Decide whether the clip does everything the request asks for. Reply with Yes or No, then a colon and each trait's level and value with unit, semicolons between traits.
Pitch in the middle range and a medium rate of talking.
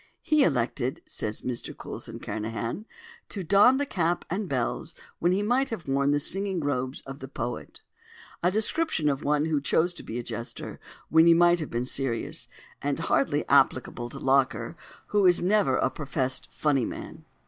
Yes: medium, 150 Hz; average, 175 wpm